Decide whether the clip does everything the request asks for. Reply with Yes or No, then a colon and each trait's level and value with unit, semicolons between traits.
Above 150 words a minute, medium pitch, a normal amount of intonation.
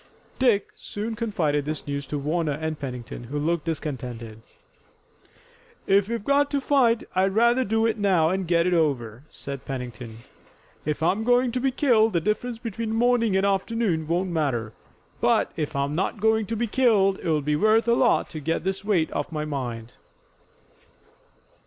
No: average, 170 wpm; medium, 180 Hz; wide, 7.2 semitones